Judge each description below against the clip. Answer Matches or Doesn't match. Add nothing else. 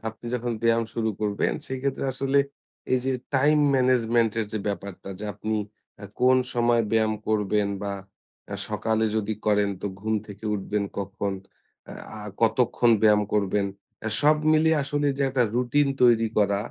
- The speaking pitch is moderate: Doesn't match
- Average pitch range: Matches